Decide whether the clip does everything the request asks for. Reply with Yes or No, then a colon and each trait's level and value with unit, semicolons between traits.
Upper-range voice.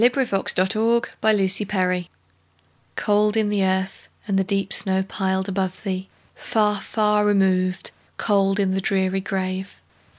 Yes: high, 195 Hz